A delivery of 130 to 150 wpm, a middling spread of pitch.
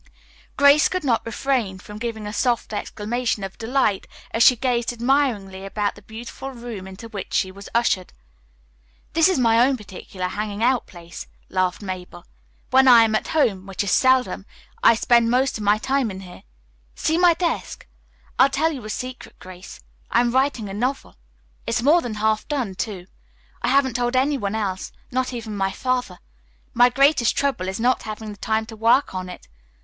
No: average, 185 wpm; average, 4.3 semitones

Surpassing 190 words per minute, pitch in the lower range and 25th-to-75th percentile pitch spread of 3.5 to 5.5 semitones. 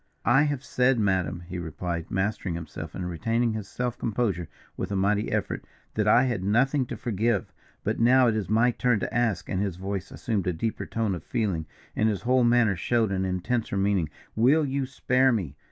Yes: average, 200 wpm; low, 110 Hz; average, 4.4 semitones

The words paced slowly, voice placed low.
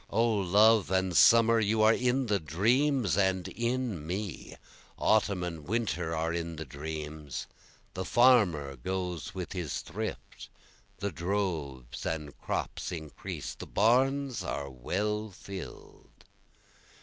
Yes: slow, 125 wpm; very low, 95 Hz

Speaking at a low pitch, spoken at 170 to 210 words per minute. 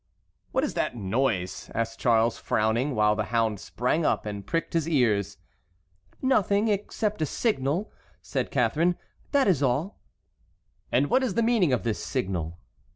No: low, 130 Hz; average, 155 wpm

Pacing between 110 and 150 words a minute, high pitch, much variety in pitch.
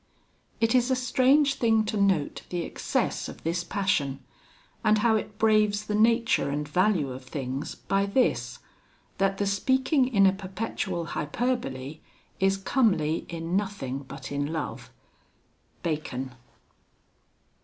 Yes: slow, 135 wpm; high, 195 Hz; wide, 6.4 semitones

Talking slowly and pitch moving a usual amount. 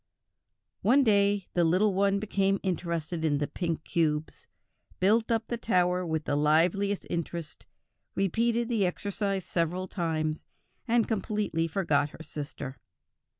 Yes: slow, 130 wpm; average, 4.0 semitones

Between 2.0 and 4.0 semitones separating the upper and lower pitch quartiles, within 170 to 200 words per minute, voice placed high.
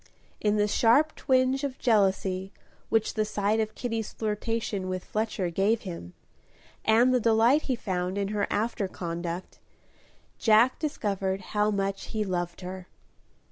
No: average, 3.2 semitones; average, 140 wpm; high, 210 Hz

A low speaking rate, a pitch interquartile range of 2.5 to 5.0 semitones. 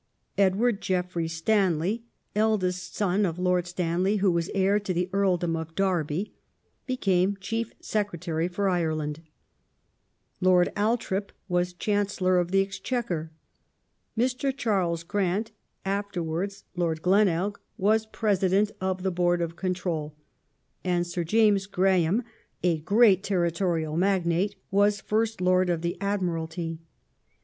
Yes: slow, 125 wpm; average, 2.8 semitones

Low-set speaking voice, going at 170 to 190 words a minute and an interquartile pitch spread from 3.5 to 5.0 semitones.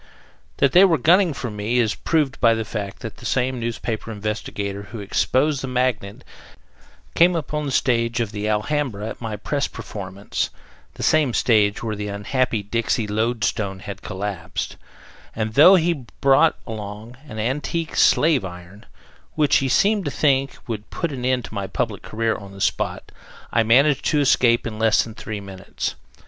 Yes: low, 115 Hz; average, 175 wpm; average, 4.6 semitones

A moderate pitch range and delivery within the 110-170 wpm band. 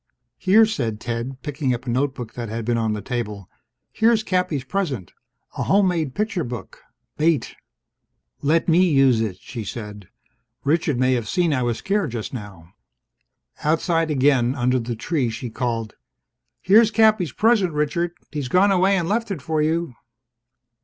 No: wide, 7.1 semitones; average, 160 wpm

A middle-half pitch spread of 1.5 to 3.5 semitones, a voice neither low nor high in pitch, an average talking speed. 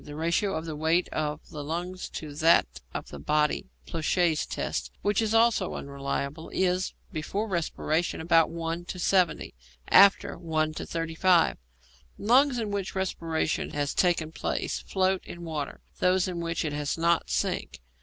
Yes: average, 3.0 semitones; medium, 165 Hz; average, 155 wpm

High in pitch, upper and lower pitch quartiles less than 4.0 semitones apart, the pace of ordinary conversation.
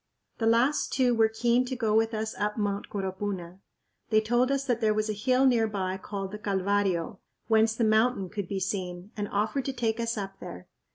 No: high, 215 Hz; average, 2.8 semitones; fast, 210 wpm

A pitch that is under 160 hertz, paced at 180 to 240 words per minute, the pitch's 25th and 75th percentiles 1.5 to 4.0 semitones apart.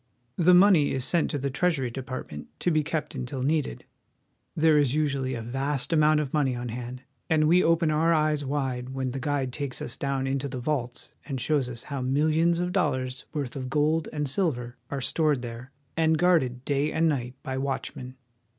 Yes: medium, 140 Hz; average, 195 wpm; average, 3.3 semitones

